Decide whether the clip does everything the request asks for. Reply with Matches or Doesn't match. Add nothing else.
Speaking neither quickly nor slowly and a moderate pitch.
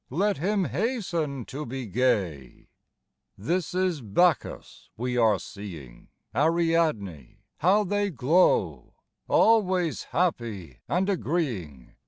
Doesn't match